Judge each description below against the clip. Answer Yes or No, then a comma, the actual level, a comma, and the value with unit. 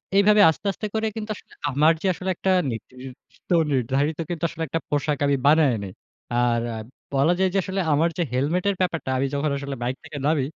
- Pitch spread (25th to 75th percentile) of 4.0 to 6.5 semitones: Yes, average, 4.9 semitones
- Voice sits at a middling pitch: Yes, medium, 150 Hz